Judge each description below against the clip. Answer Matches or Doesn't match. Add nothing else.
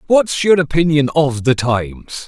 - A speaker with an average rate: Matches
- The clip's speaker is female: Doesn't match